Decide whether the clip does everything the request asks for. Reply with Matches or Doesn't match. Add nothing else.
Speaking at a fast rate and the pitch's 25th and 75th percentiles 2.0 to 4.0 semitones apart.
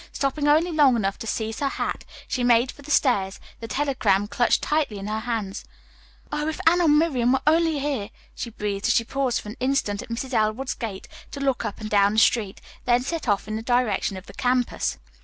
Doesn't match